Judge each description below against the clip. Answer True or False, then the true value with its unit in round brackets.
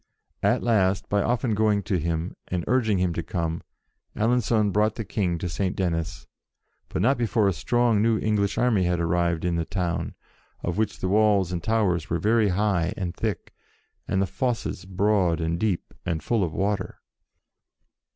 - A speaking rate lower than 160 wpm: False (175 wpm)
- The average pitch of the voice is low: True (95 Hz)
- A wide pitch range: False (3.9 semitones)